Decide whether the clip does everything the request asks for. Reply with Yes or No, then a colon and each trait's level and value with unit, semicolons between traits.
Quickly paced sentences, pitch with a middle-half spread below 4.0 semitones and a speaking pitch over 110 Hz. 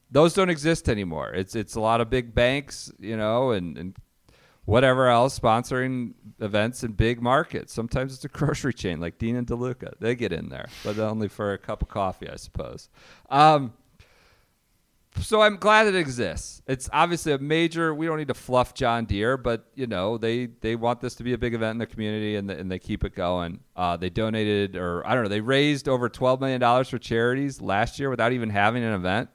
Yes: fast, 215 wpm; average, 3.6 semitones; low, 120 Hz